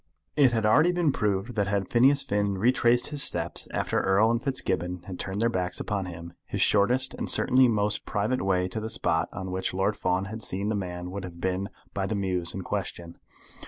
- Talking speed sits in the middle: No, fast, 210 wpm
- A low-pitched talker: Yes, low, 100 Hz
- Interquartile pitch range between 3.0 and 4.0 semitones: Yes, average, 3.7 semitones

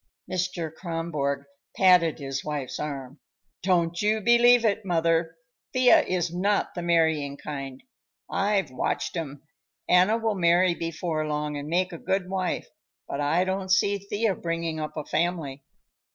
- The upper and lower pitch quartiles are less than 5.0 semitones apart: Yes, average, 3.7 semitones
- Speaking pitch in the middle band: Yes, medium, 170 Hz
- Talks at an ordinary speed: Yes, average, 145 wpm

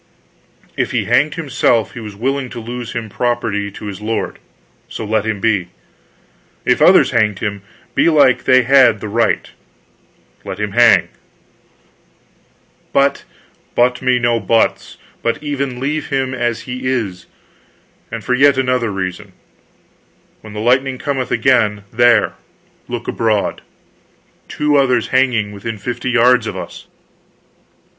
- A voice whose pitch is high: No, low, 120 Hz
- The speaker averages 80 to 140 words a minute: Yes, slow, 135 wpm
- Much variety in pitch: No, average, 3.2 semitones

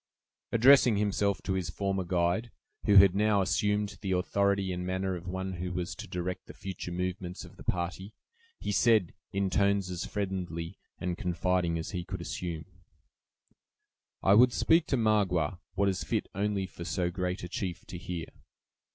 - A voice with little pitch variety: Yes, narrow, 2.1 semitones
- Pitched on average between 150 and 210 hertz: No, very low, 95 Hz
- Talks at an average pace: Yes, average, 170 wpm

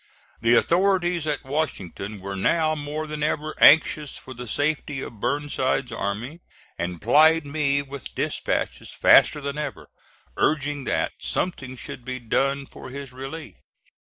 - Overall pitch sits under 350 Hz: Yes, medium, 140 Hz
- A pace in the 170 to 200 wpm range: No, average, 140 wpm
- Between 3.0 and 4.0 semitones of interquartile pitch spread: Yes, average, 3.4 semitones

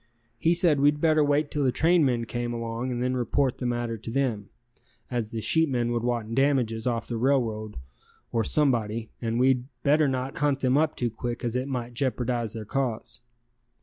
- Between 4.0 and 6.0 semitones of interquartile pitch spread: No, average, 3.0 semitones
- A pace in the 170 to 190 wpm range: Yes, average, 185 wpm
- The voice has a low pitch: Yes, low, 125 Hz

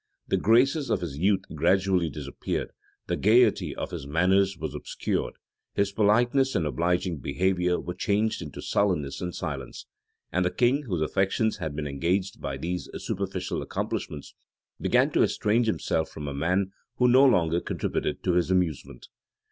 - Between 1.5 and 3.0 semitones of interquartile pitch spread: No, average, 4.1 semitones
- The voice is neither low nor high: No, very low, 90 Hz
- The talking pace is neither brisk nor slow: Yes, average, 155 wpm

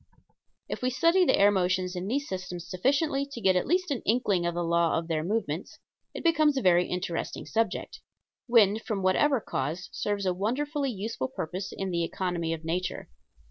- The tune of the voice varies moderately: No, wide, 6.1 semitones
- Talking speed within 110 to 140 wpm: No, average, 185 wpm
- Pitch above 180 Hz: Yes, high, 190 Hz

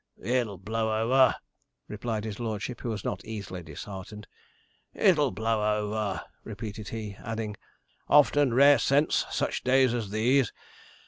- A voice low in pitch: Yes, low, 110 Hz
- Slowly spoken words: Yes, slow, 130 wpm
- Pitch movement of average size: Yes, average, 3.1 semitones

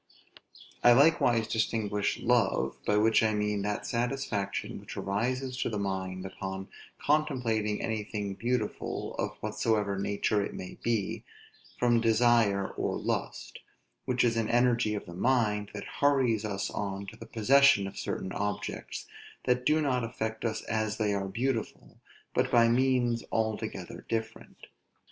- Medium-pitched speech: No, low, 110 Hz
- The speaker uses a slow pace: No, average, 145 wpm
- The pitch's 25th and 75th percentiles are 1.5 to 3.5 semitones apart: Yes, average, 2.9 semitones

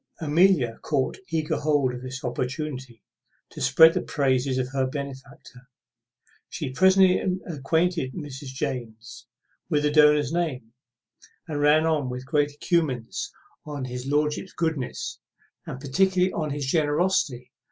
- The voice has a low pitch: No, medium, 145 Hz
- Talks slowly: Yes, slow, 130 wpm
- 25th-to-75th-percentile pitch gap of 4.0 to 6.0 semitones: No, average, 3.5 semitones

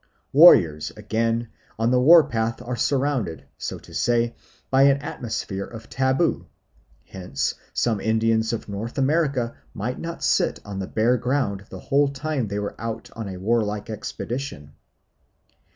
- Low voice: Yes, low, 115 Hz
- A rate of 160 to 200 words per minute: No, average, 150 wpm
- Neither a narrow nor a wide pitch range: Yes, average, 4.3 semitones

